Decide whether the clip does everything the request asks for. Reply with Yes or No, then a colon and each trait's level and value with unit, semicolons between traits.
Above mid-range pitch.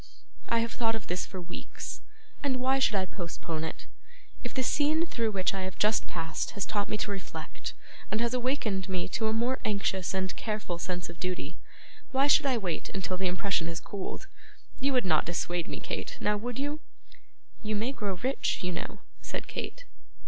Yes: high, 205 Hz